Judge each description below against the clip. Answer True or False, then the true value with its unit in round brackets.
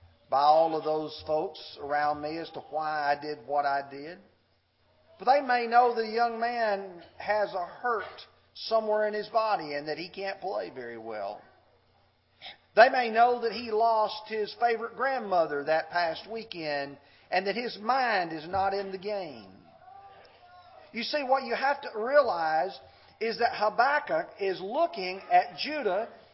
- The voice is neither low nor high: False (200 Hz)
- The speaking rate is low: False (160 wpm)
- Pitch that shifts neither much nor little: False (7.5 semitones)